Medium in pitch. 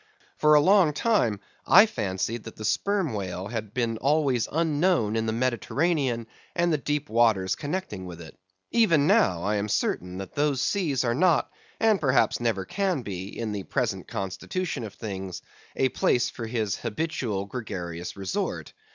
No: low, 120 Hz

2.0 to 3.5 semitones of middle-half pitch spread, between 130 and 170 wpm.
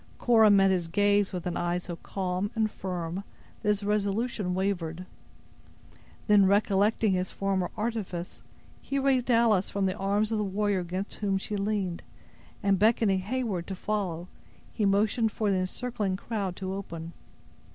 Yes: narrow, 2.4 semitones; average, 155 wpm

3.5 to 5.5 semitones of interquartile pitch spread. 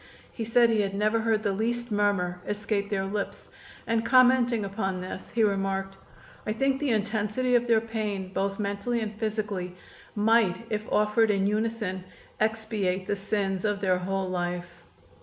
No: narrow, 2.5 semitones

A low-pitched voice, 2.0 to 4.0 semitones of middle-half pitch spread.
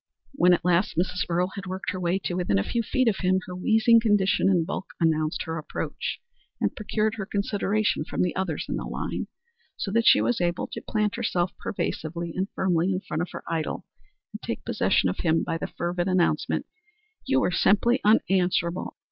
No: medium, 185 Hz; average, 3.2 semitones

